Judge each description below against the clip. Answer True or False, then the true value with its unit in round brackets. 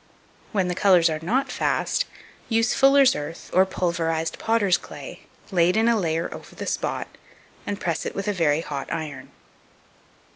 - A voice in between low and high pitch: True (180 Hz)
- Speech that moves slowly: False (160 wpm)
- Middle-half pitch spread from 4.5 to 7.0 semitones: True (5.0 semitones)